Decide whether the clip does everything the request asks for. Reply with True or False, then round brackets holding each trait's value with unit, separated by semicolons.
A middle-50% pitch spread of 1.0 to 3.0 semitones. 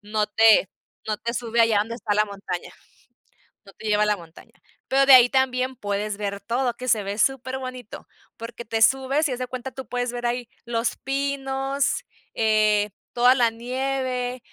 False (3.4 semitones)